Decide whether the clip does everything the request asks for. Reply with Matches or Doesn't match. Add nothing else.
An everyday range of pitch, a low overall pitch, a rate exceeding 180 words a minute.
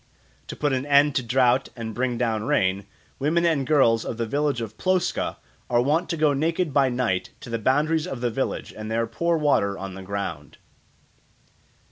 Matches